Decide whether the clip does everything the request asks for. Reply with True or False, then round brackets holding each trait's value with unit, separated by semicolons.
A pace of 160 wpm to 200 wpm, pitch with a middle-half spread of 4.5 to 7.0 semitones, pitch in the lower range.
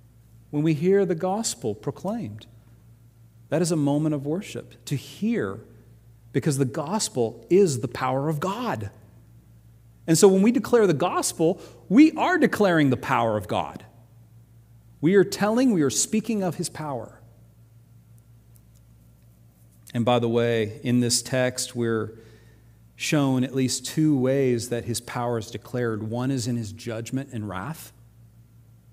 False (145 wpm; 5.1 semitones; 120 Hz)